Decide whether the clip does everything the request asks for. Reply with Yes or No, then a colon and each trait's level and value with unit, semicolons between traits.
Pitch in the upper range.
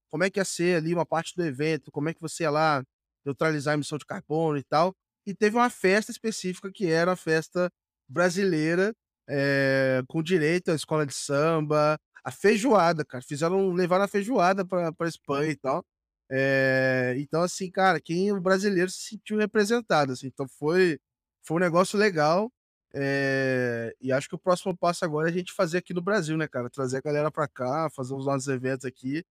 No: medium, 160 Hz